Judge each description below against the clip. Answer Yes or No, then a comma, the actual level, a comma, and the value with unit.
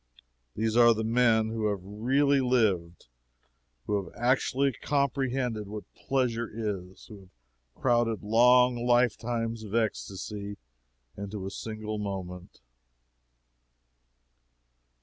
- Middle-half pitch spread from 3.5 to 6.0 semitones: No, average, 3.0 semitones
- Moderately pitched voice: No, low, 110 Hz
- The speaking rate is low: Yes, slow, 105 wpm